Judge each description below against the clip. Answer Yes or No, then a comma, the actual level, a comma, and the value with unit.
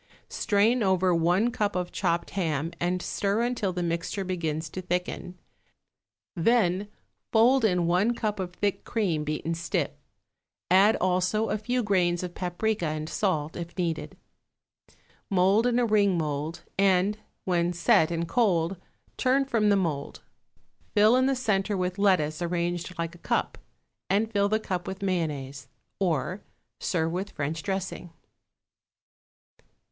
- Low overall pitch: No, medium, 185 Hz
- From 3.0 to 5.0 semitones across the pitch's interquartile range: Yes, average, 3.4 semitones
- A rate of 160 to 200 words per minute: No, average, 140 wpm